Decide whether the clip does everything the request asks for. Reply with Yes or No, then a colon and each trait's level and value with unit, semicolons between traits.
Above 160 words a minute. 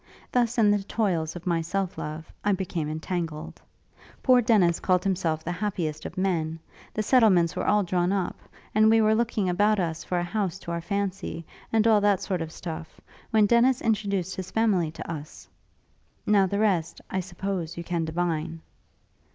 Yes: average, 180 wpm